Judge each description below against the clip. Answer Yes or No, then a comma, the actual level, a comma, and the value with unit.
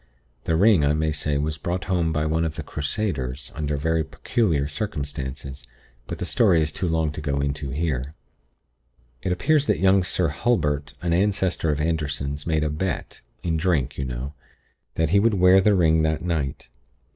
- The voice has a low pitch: Yes, very low, 80 Hz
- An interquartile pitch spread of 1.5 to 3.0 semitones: No, average, 3.6 semitones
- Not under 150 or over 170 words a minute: No, average, 180 wpm